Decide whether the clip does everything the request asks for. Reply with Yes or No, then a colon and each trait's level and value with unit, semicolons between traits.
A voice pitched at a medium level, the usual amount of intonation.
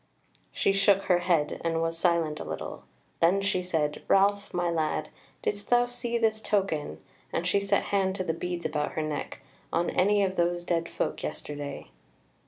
Yes: medium, 175 Hz; average, 3.4 semitones